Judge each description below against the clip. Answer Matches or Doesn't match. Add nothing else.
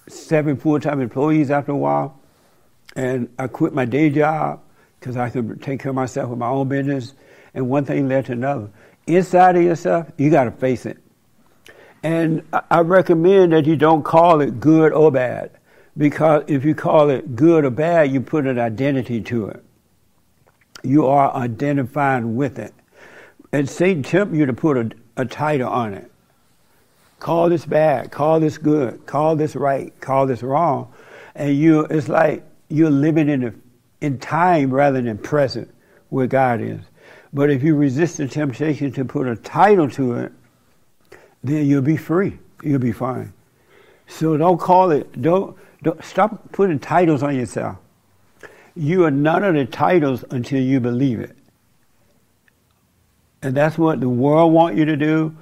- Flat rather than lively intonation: Doesn't match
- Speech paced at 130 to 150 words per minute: Doesn't match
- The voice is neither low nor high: Matches